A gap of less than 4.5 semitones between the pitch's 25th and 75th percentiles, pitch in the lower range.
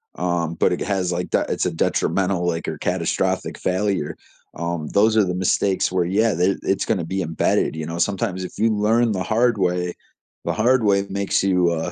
Yes: average, 2.8 semitones; very low, 95 Hz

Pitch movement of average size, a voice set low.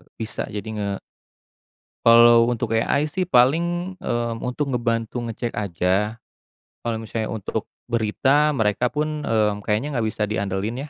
Yes: average, 3.7 semitones; low, 115 Hz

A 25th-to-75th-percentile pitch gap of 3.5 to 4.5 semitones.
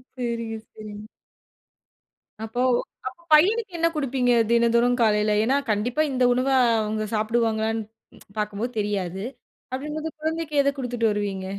Yes: average, 4.0 semitones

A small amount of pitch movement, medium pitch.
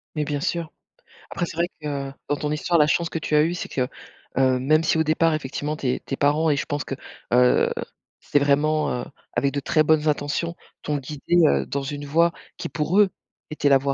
Yes: narrow, 2.2 semitones; medium, 150 Hz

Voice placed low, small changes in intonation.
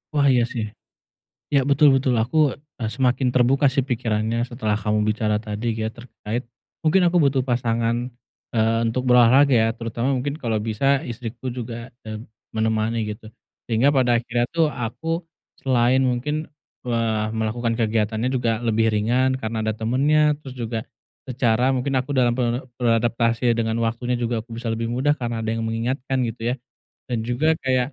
Yes: low, 120 Hz; narrow, 2.3 semitones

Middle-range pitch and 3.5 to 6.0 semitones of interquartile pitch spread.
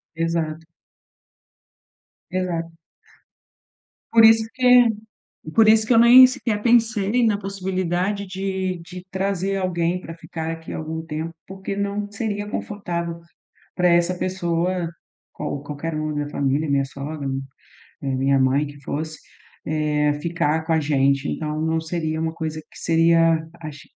Yes: medium, 170 Hz; average, 4.0 semitones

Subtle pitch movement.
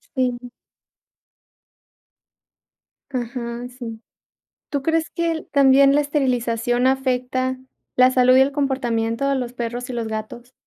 Yes: narrow, 2.2 semitones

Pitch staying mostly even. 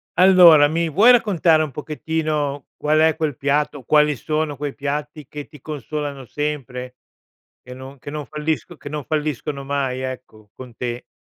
Yes: narrow, 2.2 semitones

